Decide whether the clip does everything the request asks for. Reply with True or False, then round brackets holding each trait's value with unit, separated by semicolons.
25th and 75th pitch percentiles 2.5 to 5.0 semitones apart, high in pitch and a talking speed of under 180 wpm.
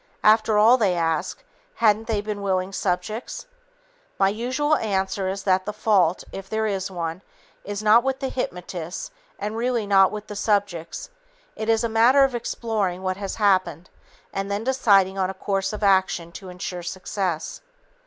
True (2.8 semitones; 200 Hz; 170 wpm)